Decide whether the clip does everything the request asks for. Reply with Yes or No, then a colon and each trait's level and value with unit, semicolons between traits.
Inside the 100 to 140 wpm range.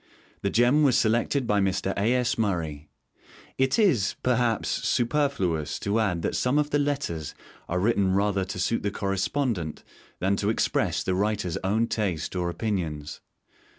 No: average, 155 wpm